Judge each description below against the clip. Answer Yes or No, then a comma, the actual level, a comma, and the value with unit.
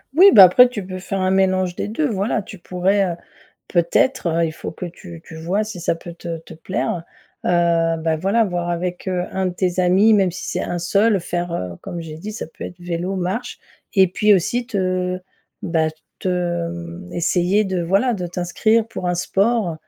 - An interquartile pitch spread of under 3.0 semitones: Yes, narrow, 2.4 semitones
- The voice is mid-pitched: Yes, medium, 180 Hz